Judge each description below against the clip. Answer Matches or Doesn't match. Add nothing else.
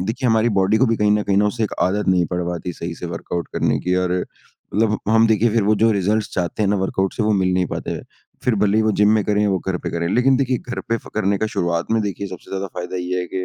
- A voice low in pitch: Matches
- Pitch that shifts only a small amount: Doesn't match